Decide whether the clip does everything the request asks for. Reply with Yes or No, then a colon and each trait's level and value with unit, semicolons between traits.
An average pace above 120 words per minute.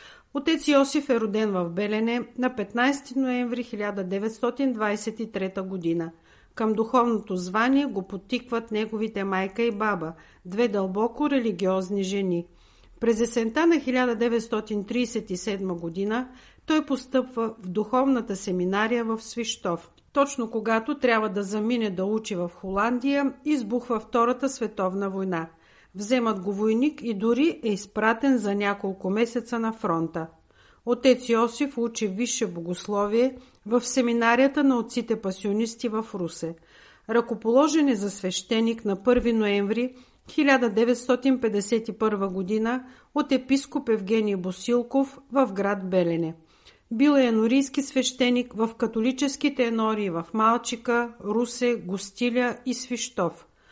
No: slow, 115 wpm